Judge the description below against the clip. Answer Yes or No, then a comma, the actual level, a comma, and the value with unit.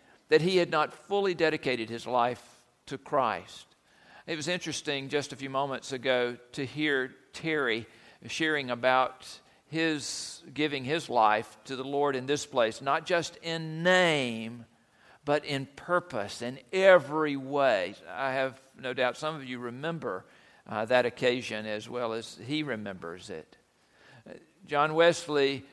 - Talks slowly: No, average, 145 wpm